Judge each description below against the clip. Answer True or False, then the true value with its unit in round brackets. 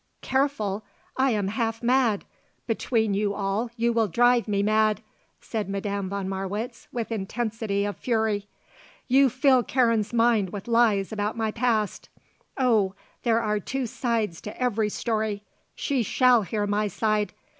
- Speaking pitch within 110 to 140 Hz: False (220 Hz)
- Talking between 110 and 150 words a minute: True (145 wpm)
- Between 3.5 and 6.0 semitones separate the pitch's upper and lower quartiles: False (2.7 semitones)